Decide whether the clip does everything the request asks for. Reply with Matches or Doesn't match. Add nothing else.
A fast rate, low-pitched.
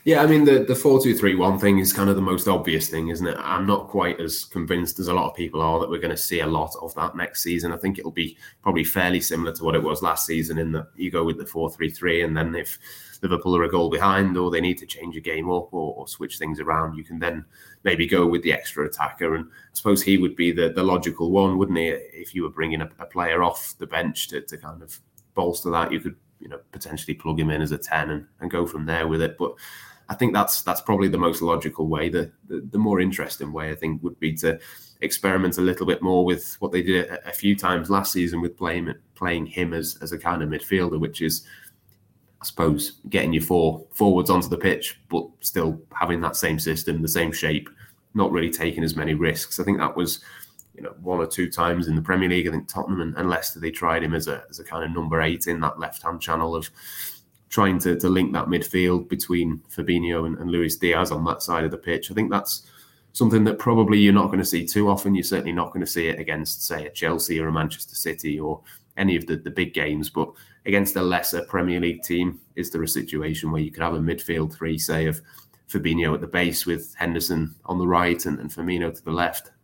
Matches